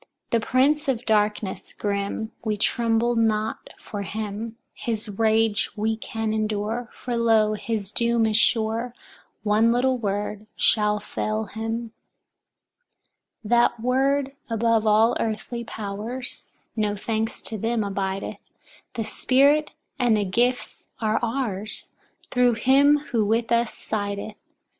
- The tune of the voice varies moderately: No, narrow, 2.0 semitones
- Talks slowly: Yes, slow, 125 wpm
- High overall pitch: Yes, high, 225 Hz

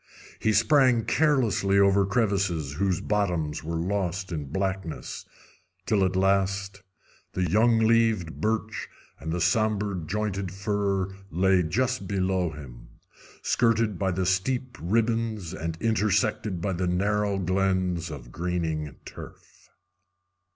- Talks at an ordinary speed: No, slow, 120 wpm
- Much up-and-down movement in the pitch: No, average, 3.3 semitones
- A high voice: No, very low, 95 Hz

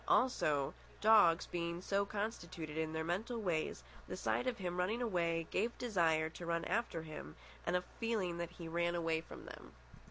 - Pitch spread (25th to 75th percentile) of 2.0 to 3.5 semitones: No, average, 4.2 semitones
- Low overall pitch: No, medium, 175 Hz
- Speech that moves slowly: No, average, 180 wpm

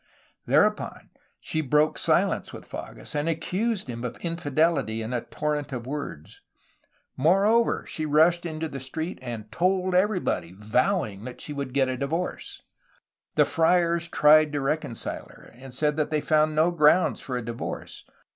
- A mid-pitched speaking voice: Yes, medium, 150 Hz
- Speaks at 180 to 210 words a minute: No, average, 160 wpm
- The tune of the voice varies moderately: Yes, average, 4.6 semitones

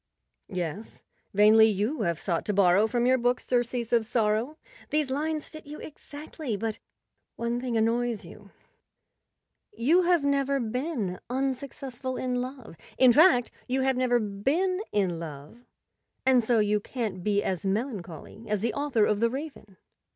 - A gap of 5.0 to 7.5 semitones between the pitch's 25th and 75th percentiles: No, average, 4.2 semitones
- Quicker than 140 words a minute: Yes, average, 150 wpm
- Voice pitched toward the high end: Yes, high, 240 Hz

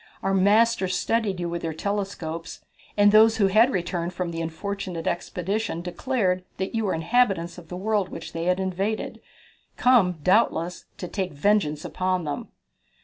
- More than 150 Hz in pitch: Yes, medium, 185 Hz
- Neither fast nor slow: Yes, average, 160 wpm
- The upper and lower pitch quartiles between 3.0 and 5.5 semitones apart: Yes, average, 3.3 semitones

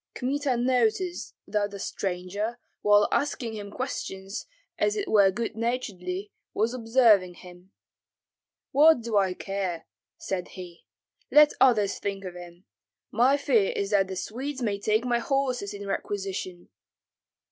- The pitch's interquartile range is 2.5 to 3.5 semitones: No, average, 4.5 semitones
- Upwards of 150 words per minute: No, slow, 135 wpm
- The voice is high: Yes, high, 210 Hz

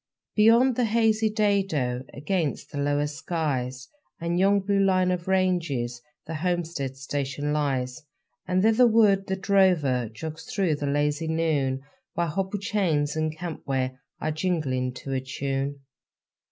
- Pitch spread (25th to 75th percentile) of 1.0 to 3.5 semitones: No, wide, 5.5 semitones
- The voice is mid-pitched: Yes, medium, 160 Hz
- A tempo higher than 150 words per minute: No, average, 140 wpm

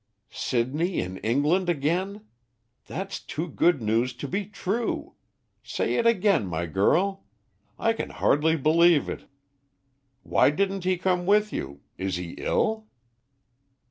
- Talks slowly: Yes, slow, 130 wpm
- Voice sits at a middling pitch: Yes, medium, 170 Hz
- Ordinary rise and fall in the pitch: No, wide, 7.4 semitones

